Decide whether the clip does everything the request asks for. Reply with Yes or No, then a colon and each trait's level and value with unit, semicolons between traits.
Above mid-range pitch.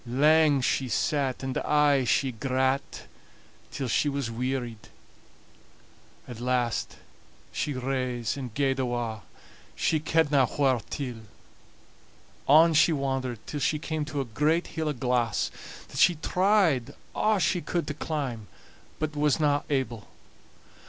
No: low, 135 Hz